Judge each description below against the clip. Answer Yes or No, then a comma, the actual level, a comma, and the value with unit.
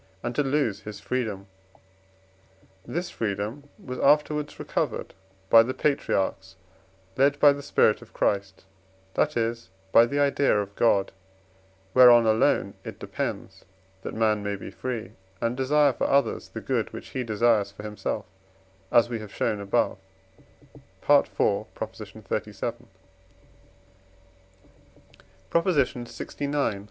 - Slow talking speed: Yes, slow, 125 wpm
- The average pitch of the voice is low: Yes, low, 120 Hz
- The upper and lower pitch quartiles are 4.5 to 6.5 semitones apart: Yes, average, 5.1 semitones